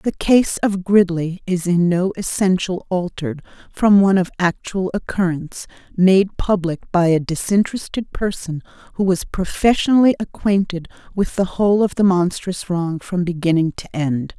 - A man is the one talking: No, female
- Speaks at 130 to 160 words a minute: Yes, average, 145 wpm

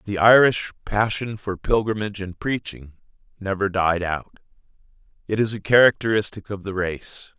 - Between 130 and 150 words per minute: Yes, average, 140 wpm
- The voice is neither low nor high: No, low, 100 Hz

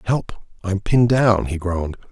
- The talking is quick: No, average, 170 wpm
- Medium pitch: No, low, 100 Hz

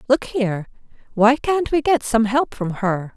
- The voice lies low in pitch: No, high, 240 Hz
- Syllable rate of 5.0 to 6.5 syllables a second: No, 4.4 syllables/s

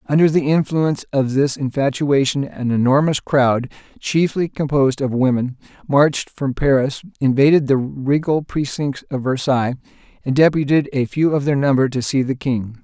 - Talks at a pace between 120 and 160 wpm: Yes, average, 155 wpm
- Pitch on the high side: No, medium, 140 Hz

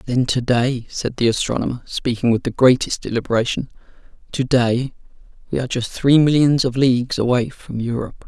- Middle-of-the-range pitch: No, low, 125 Hz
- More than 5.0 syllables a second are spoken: Yes, 5.4 syllables/s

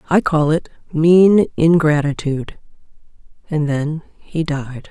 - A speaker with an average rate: No, slow, 110 wpm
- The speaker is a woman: Yes, female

